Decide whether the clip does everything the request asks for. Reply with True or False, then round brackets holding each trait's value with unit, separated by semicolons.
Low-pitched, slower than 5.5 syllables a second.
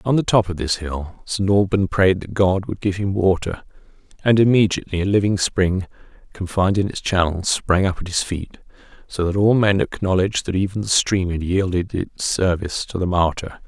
True (95 Hz; 5.2 syllables/s)